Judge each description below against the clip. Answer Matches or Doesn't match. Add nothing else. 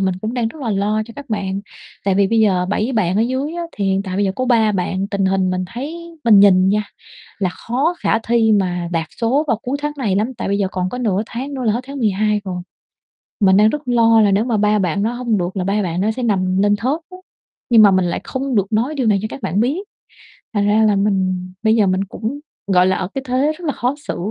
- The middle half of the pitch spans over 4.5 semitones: Doesn't match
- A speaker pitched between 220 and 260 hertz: Doesn't match